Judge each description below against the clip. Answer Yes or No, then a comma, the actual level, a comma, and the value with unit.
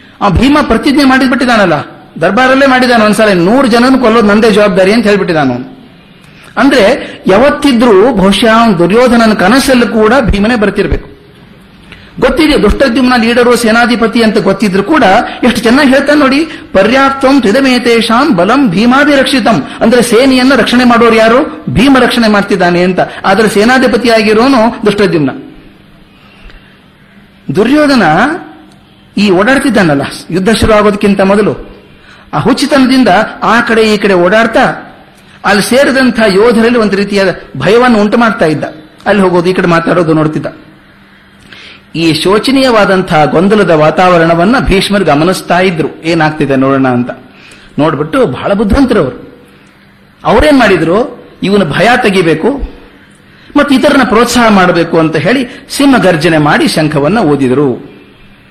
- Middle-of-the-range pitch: No, high, 220 Hz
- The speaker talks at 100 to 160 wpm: Yes, fast, 105 wpm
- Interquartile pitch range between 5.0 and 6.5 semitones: Yes, average, 5.3 semitones